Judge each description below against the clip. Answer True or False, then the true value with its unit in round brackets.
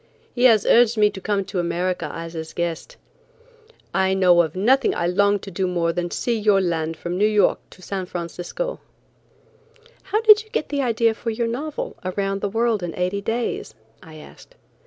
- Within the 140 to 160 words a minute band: False (200 wpm)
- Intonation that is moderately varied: True (4.7 semitones)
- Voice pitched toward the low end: False (195 Hz)